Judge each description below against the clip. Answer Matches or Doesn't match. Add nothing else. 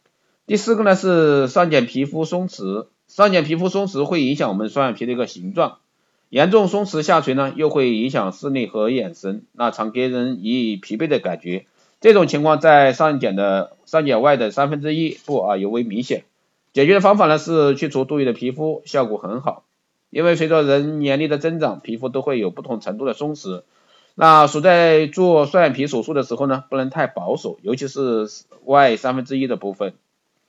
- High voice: Doesn't match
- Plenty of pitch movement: Doesn't match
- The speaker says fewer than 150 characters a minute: Doesn't match